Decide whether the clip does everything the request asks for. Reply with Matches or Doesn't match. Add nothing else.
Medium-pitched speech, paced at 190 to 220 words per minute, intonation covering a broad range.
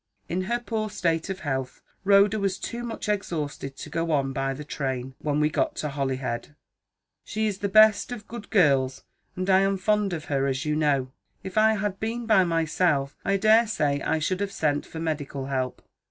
Matches